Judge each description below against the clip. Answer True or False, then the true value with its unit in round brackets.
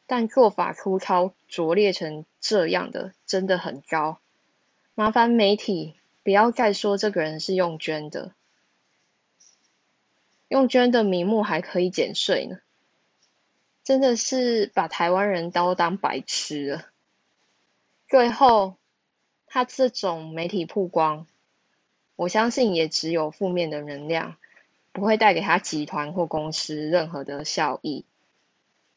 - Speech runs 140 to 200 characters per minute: True (180 characters per minute)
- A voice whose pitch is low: False (180 Hz)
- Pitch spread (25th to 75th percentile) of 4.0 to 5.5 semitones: True (5.1 semitones)